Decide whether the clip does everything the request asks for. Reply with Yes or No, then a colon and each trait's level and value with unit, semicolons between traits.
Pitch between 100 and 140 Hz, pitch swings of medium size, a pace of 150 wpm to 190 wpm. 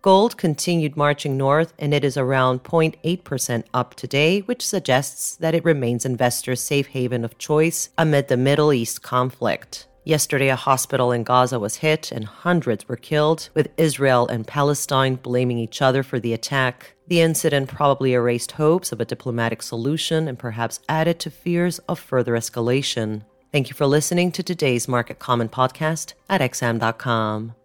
Yes: low, 135 Hz; average, 4.2 semitones; average, 165 wpm